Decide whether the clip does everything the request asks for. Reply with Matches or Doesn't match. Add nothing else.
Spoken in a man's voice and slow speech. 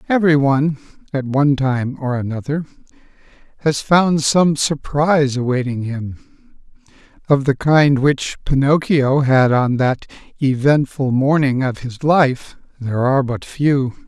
Matches